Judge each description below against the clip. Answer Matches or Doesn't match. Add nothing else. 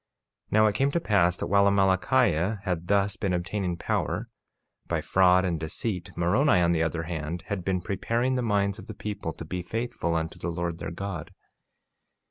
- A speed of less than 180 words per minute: Doesn't match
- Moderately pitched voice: Doesn't match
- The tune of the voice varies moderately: Matches